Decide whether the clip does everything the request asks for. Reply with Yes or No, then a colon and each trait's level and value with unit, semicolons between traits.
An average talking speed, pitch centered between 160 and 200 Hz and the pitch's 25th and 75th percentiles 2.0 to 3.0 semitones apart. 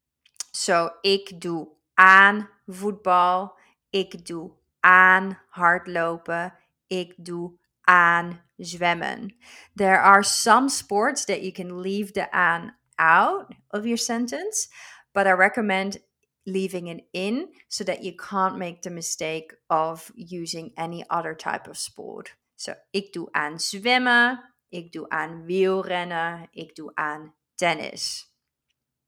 No: slow, 125 wpm; medium, 185 Hz; narrow, 2.6 semitones